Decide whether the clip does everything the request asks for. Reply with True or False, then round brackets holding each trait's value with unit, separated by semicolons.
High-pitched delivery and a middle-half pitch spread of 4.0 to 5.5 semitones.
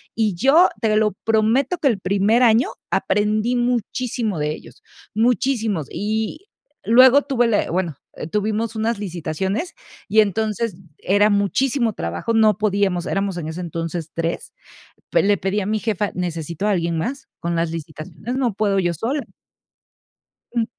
True (210 Hz; 4.3 semitones)